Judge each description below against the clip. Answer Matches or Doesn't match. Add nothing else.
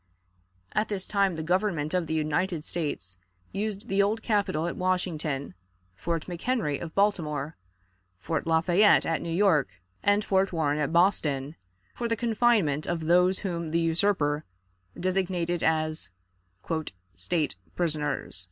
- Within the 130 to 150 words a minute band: Matches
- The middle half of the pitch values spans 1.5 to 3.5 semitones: Doesn't match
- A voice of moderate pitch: Matches